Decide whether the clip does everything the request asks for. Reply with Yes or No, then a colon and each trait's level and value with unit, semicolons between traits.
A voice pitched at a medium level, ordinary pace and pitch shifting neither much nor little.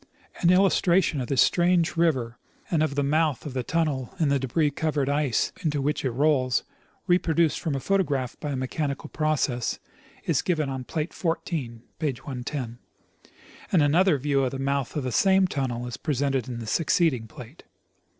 Yes: medium, 145 Hz; average, 175 wpm; average, 3.8 semitones